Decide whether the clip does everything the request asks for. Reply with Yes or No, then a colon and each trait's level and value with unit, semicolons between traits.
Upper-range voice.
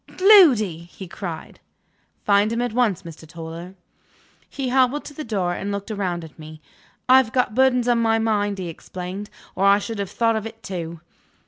Yes: high, 205 Hz